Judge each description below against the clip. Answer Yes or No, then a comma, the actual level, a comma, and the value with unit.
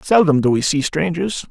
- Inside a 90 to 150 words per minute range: No, average, 200 wpm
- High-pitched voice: No, medium, 160 Hz